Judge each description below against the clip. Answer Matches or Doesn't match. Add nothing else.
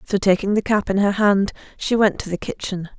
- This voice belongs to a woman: Matches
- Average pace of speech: Doesn't match